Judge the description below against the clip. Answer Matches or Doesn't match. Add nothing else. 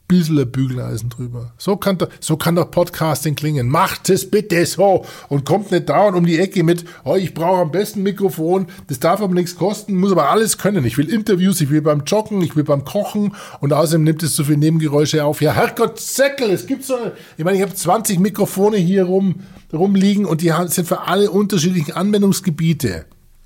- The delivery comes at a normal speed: Doesn't match